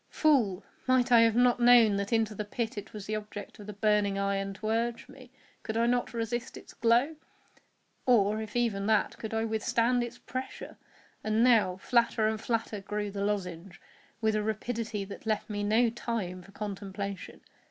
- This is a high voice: Yes, high, 215 Hz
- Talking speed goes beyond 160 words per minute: Yes, average, 180 wpm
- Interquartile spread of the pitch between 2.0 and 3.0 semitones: Yes, narrow, 2.5 semitones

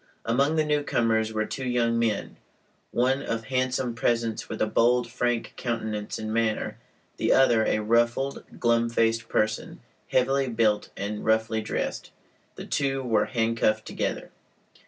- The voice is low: Yes, low, 115 Hz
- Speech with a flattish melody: Yes, narrow, 2.1 semitones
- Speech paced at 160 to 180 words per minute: No, average, 140 wpm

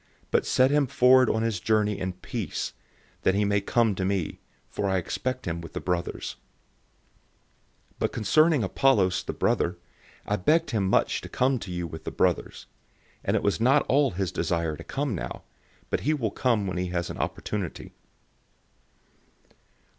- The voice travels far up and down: Yes, wide, 5.8 semitones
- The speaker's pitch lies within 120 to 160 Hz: No, low, 100 Hz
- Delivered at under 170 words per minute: No, average, 175 wpm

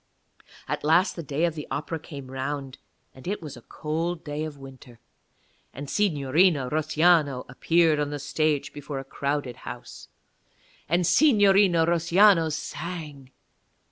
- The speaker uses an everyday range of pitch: Yes, average, 3.5 semitones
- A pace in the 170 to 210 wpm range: No, average, 140 wpm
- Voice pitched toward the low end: No, medium, 150 Hz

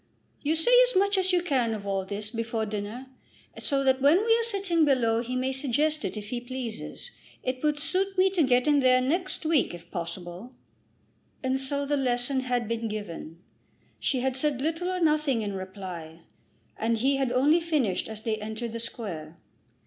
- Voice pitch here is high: Yes, very high, 255 Hz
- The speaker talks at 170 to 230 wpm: Yes, average, 190 wpm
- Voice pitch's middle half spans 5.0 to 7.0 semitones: Yes, wide, 5.6 semitones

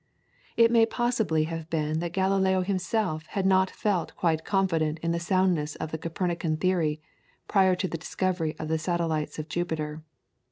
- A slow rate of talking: No, average, 165 wpm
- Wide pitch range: No, average, 3.2 semitones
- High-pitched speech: No, medium, 170 Hz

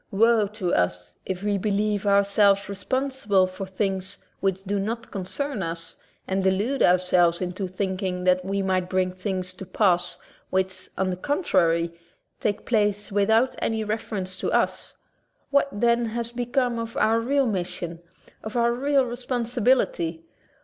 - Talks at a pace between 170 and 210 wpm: No, average, 145 wpm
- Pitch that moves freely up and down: No, average, 3.7 semitones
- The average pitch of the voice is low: No, high, 200 Hz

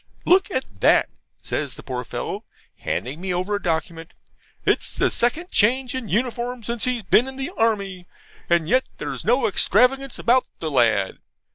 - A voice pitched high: Yes, high, 230 Hz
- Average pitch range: No, wide, 6.2 semitones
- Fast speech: No, average, 165 wpm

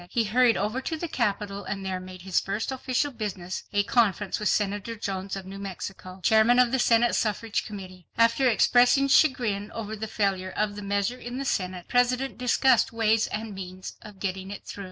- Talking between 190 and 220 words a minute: Yes, average, 195 wpm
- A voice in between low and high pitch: No, high, 210 Hz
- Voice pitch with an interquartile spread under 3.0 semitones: No, average, 3.7 semitones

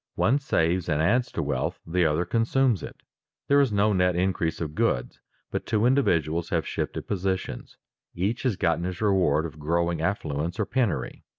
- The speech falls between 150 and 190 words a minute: Yes, average, 175 wpm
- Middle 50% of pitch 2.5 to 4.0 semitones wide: No, average, 4.5 semitones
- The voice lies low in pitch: Yes, very low, 90 Hz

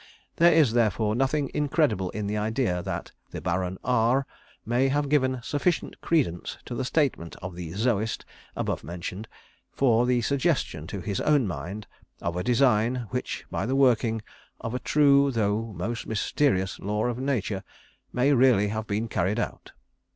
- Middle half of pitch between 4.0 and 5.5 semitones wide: Yes, average, 4.8 semitones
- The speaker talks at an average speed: Yes, average, 160 wpm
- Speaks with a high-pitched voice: No, low, 115 Hz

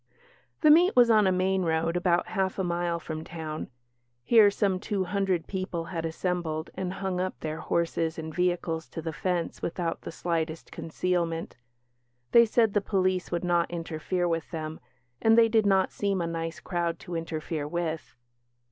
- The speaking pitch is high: No, medium, 175 Hz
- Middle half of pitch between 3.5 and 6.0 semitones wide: No, narrow, 2.6 semitones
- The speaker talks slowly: No, average, 175 wpm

